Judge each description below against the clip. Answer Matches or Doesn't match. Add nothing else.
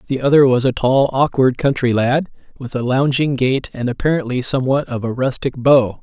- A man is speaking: Matches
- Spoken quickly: Doesn't match